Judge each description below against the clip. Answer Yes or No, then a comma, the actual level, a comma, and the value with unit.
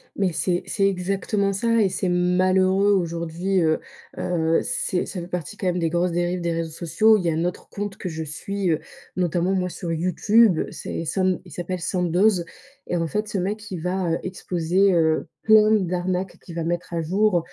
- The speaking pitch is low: No, medium, 180 Hz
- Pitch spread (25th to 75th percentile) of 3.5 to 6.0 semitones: No, narrow, 2.4 semitones